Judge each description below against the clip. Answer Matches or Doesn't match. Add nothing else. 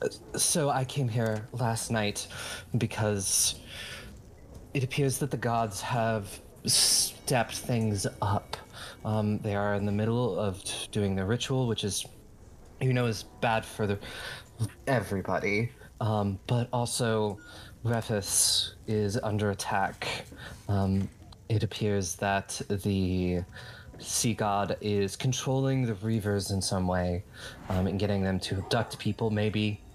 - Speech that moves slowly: Matches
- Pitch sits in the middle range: Doesn't match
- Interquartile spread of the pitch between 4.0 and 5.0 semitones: Doesn't match